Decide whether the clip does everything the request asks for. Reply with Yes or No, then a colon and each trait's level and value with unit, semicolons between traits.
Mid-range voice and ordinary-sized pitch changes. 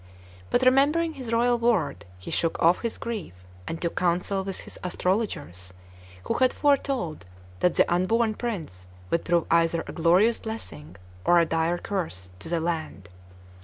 No: medium, 175 Hz; wide, 6.0 semitones